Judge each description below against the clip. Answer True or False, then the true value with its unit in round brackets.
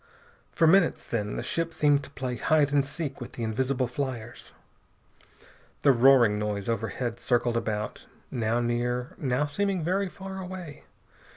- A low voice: True (130 Hz)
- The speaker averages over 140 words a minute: True (150 wpm)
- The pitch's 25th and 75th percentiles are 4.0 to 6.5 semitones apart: True (4.5 semitones)